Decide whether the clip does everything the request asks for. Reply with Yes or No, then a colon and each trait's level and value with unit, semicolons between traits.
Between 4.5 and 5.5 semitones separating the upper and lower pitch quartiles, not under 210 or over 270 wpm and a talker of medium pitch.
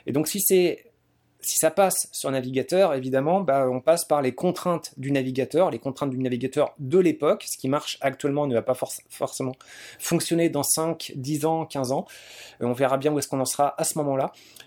No: average, 3.5 semitones; average, 215 wpm; medium, 145 Hz